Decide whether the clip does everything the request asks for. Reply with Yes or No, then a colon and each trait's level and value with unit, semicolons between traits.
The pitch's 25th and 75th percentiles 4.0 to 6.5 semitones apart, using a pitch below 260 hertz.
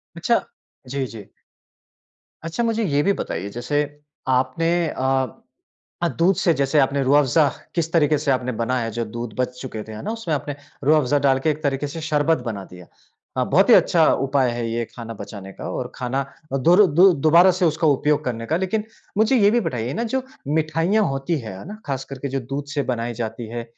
Yes: average, 4.9 semitones; medium, 140 Hz